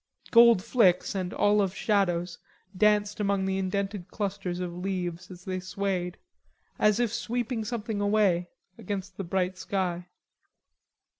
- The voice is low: No, high, 195 Hz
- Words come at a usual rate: No, slow, 130 wpm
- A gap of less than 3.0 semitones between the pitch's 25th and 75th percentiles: Yes, narrow, 2.4 semitones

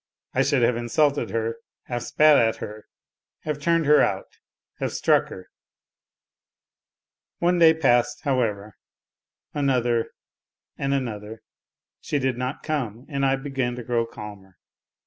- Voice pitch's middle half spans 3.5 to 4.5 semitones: Yes, average, 3.8 semitones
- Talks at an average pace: No, slow, 130 wpm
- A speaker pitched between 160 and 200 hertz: No, low, 125 Hz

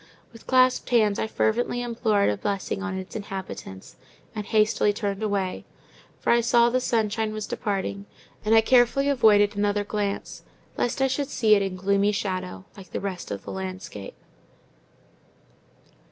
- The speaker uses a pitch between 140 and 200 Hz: No, high, 210 Hz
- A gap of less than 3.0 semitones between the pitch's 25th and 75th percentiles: Yes, narrow, 2.6 semitones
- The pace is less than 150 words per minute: No, average, 155 wpm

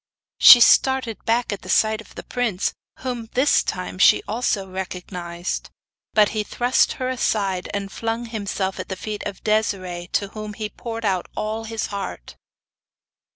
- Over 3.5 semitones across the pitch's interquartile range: No, average, 3.1 semitones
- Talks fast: No, average, 160 wpm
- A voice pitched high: Yes, high, 215 Hz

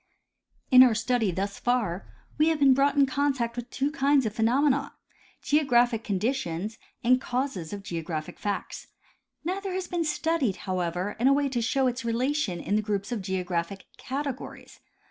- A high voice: Yes, high, 245 Hz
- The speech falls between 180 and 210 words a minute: No, average, 165 wpm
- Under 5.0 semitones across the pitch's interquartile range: No, wide, 5.6 semitones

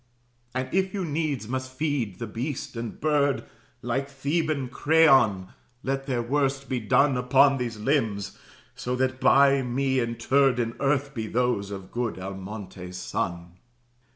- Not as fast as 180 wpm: Yes, average, 145 wpm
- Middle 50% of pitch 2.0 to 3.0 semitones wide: No, average, 3.5 semitones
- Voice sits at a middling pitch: No, low, 130 Hz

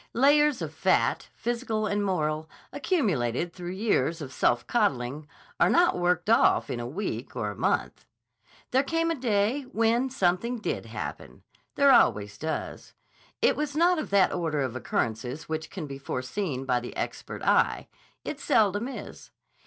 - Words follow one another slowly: No, average, 160 wpm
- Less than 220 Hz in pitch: Yes, high, 190 Hz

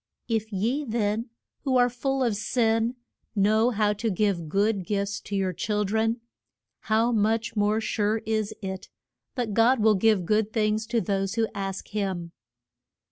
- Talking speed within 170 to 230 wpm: No, average, 160 wpm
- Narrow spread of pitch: Yes, narrow, 2.0 semitones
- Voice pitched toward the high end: Yes, high, 215 Hz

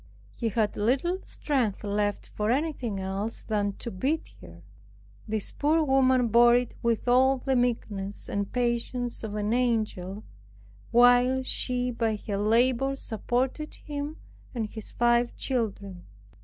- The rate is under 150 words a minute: Yes, slow, 135 wpm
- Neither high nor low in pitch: No, high, 235 Hz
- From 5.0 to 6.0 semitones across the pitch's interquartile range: No, average, 3.4 semitones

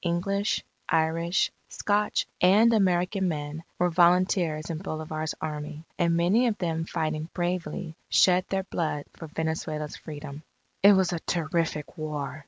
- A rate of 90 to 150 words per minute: Yes, slow, 135 wpm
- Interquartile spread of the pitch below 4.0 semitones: Yes, average, 2.8 semitones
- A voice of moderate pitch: Yes, medium, 170 Hz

